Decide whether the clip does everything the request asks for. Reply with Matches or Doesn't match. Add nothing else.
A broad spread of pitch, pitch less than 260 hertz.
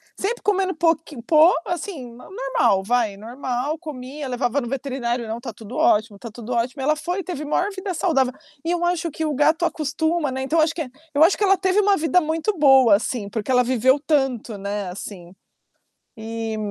Doesn't match